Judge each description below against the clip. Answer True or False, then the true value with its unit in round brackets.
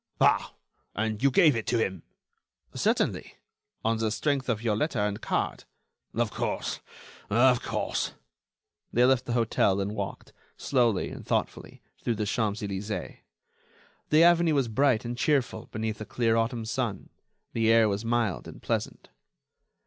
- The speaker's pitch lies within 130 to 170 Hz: False (115 Hz)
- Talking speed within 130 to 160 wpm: True (150 wpm)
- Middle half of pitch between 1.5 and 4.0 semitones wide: True (2.8 semitones)